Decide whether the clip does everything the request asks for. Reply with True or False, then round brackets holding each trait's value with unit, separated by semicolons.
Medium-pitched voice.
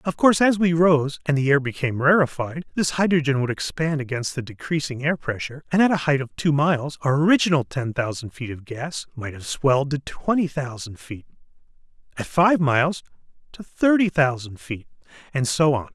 True (145 Hz)